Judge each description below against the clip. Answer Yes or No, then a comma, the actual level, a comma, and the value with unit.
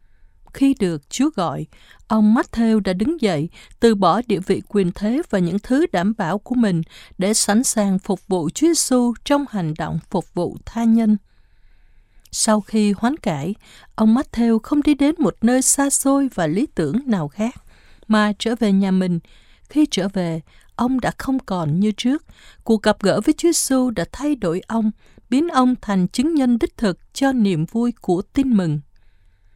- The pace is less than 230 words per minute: Yes, average, 185 wpm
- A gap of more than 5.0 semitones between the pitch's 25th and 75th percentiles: Yes, wide, 5.6 semitones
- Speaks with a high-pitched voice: Yes, high, 215 Hz